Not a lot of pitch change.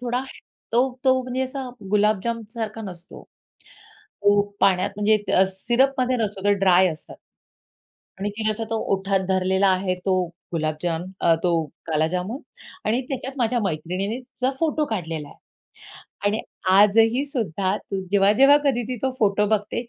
No: average, 4.6 semitones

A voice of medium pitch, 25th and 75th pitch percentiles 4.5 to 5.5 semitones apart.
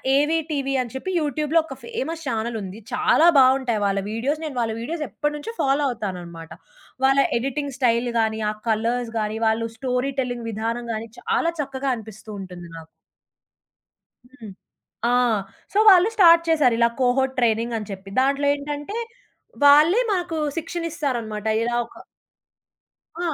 No: very high, 255 Hz; average, 4.8 semitones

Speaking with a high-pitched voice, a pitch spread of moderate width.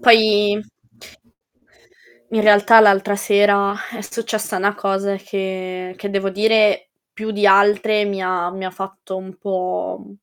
No: high, 200 Hz; narrow, 1.7 semitones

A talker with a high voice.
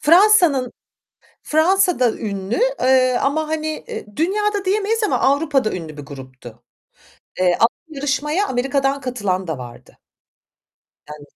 Yes: very high, 270 Hz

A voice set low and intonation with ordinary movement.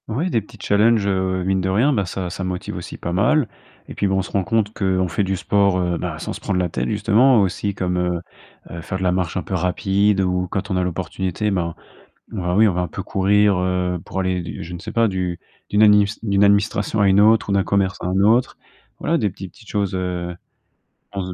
No: very low, 95 Hz; narrow, 2.2 semitones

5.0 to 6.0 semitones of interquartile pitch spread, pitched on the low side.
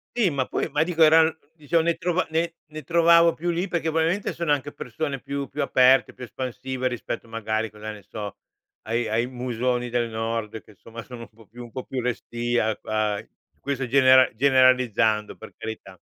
Yes: average, 5.3 semitones; low, 130 Hz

